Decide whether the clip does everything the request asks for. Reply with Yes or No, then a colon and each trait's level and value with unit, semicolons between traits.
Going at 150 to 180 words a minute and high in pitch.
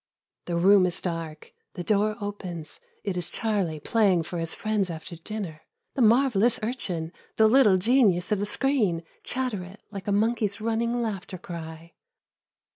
Yes: average, 160 wpm; high, 200 Hz